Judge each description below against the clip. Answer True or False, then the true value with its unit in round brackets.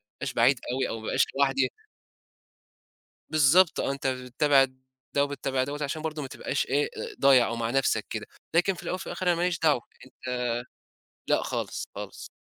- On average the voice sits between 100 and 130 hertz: False (140 Hz)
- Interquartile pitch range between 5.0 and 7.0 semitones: False (2.9 semitones)